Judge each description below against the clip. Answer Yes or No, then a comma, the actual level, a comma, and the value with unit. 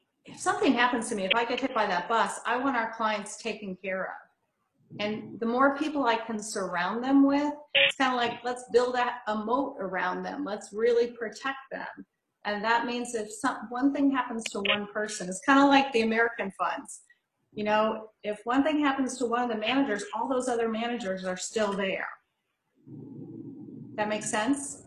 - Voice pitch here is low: No, high, 230 Hz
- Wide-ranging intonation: No, average, 3.3 semitones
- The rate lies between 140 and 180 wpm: No, average, 195 wpm